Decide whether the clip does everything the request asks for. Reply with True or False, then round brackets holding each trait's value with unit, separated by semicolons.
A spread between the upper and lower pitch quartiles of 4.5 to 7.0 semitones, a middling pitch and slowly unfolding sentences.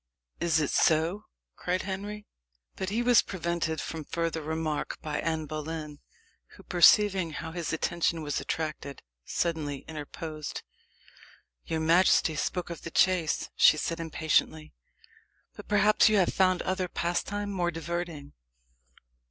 False (2.9 semitones; 165 Hz; 130 wpm)